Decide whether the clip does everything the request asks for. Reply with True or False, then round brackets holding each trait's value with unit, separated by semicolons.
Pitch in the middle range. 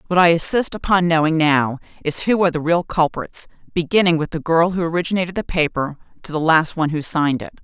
True (165 Hz)